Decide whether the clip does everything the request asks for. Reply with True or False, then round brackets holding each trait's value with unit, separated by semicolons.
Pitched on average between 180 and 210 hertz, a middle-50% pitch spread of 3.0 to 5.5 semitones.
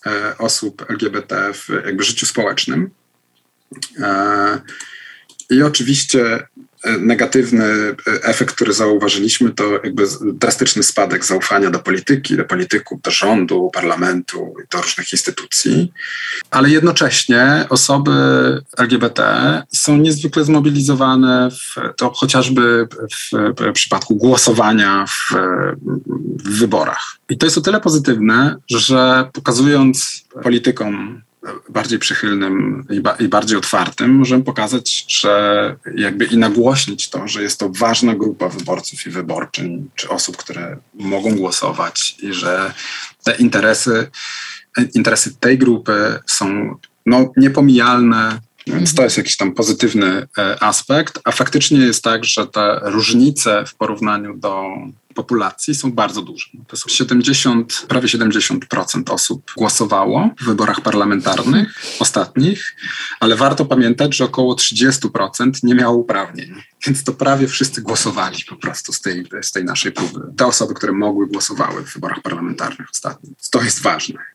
False (125 Hz; 3.7 semitones)